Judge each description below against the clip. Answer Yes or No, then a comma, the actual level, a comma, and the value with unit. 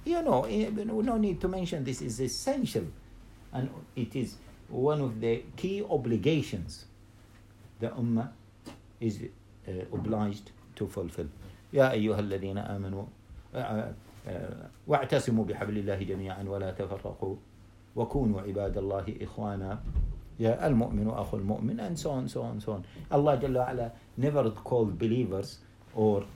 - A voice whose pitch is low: Yes, low, 110 Hz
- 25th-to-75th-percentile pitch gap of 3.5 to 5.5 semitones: Yes, average, 3.8 semitones